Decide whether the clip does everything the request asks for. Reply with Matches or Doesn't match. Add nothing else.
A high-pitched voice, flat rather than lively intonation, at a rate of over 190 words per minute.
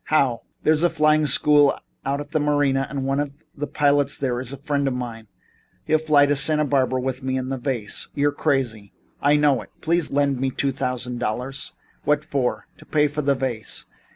Doesn't match